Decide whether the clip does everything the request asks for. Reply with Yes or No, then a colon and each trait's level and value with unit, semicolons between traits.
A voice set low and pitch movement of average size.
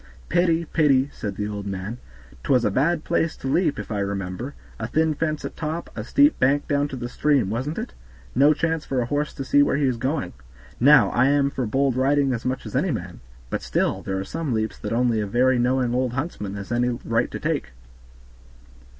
Yes: low, 130 Hz; average, 4.2 semitones